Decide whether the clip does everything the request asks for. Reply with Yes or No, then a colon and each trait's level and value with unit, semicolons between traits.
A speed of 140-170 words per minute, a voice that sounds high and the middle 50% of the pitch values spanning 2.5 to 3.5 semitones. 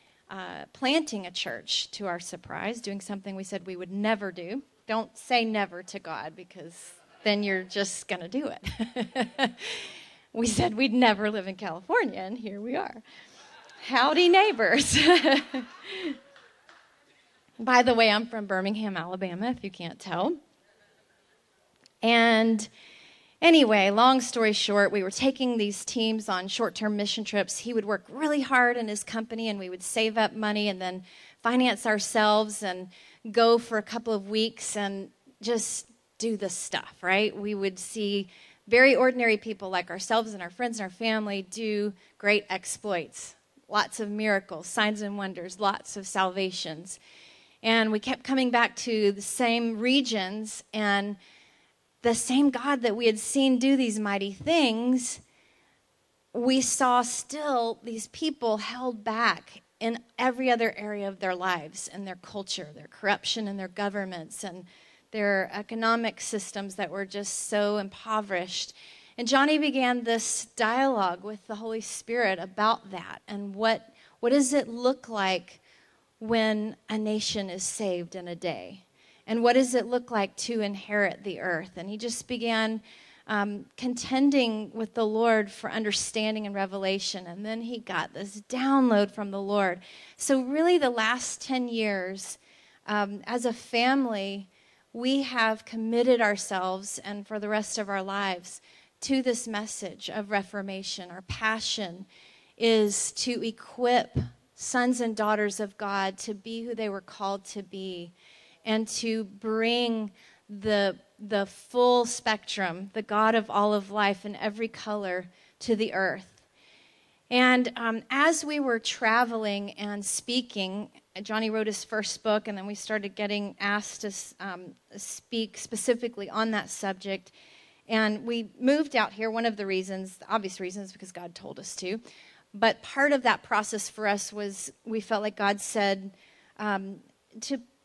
Yes: average, 155 wpm; high, 215 Hz; average, 2.9 semitones